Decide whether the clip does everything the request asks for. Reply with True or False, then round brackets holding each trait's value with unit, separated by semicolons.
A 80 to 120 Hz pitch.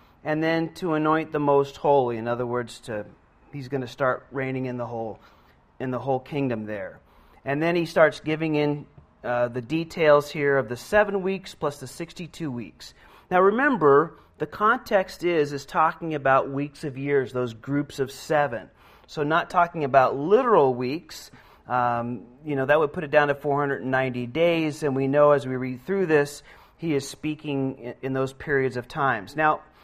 False (140 Hz)